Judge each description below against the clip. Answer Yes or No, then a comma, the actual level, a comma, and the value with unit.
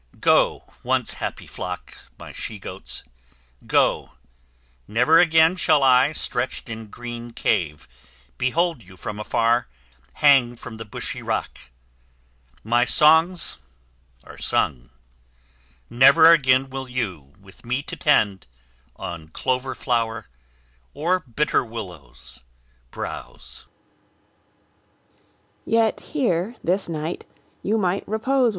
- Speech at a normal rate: No, slow, 90 wpm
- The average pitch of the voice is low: Yes, low, 120 Hz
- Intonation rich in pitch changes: No, average, 4.8 semitones